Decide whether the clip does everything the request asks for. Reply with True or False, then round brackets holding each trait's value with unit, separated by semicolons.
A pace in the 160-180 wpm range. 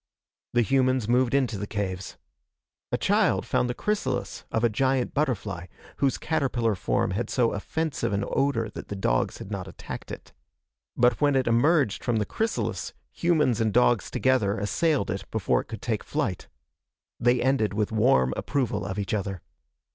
True (170 wpm)